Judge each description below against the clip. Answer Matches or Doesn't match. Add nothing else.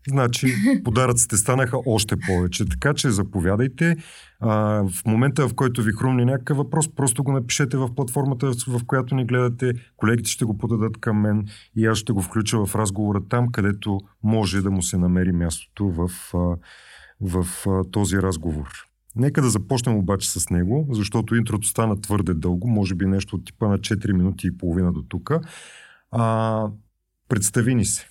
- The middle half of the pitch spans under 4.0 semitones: Doesn't match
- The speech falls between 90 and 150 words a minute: Doesn't match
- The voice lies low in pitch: Matches